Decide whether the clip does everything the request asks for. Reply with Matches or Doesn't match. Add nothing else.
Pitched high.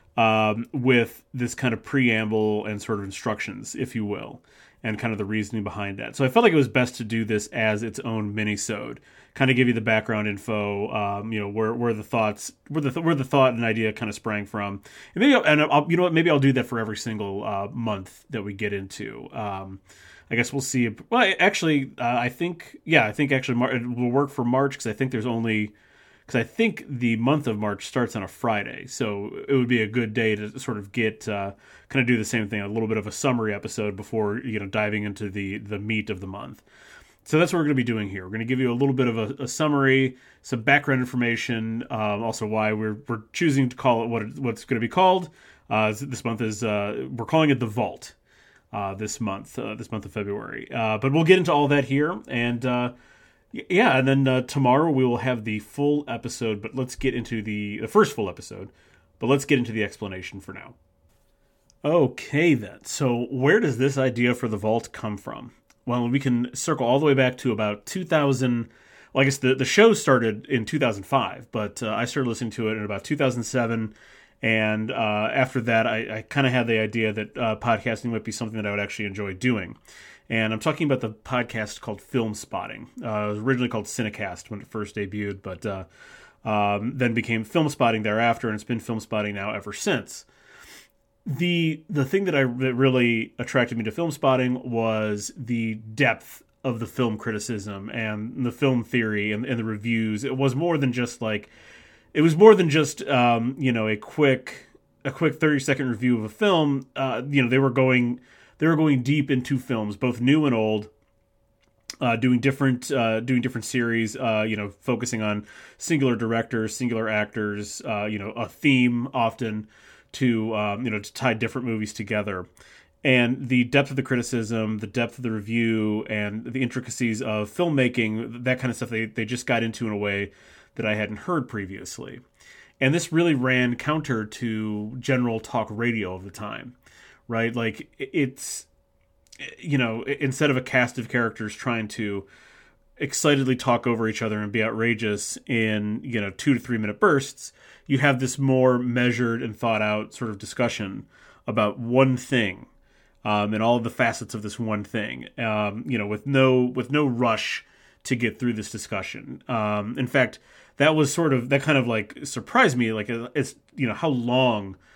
Doesn't match